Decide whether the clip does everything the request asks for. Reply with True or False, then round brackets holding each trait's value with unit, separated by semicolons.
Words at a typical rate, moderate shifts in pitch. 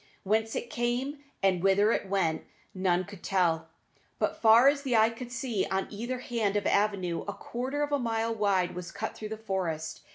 True (195 wpm; 4.0 semitones)